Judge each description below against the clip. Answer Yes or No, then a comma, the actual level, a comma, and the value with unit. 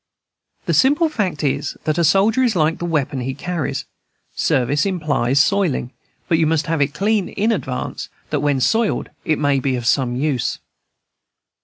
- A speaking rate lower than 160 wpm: No, average, 170 wpm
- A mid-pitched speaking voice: Yes, medium, 155 Hz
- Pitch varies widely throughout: Yes, wide, 6.0 semitones